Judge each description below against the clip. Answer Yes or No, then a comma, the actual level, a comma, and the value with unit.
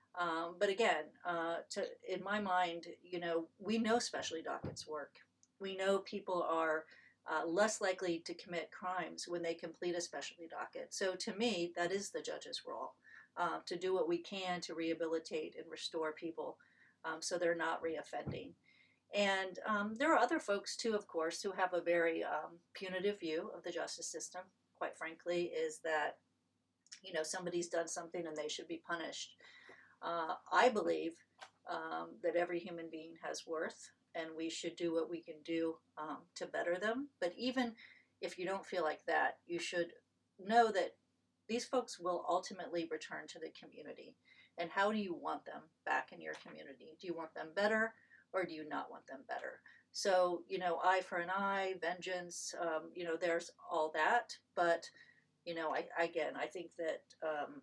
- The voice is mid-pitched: Yes, medium, 175 Hz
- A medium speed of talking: Yes, average, 185 wpm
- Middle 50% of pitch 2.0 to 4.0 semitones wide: Yes, average, 2.9 semitones